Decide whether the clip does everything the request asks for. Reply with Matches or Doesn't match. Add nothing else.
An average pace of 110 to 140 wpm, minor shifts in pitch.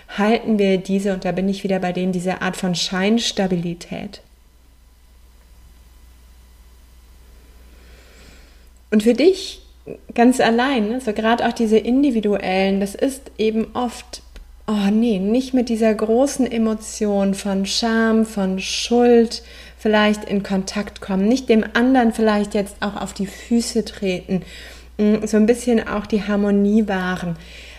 Doesn't match